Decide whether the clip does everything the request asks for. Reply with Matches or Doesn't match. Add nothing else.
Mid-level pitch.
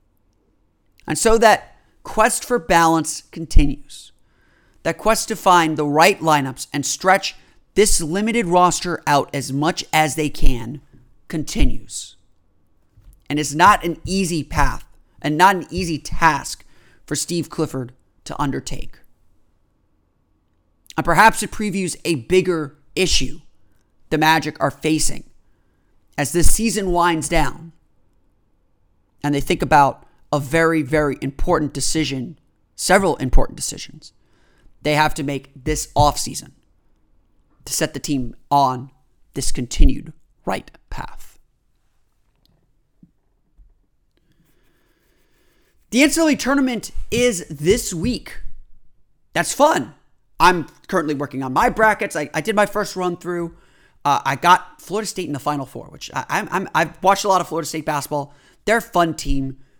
Matches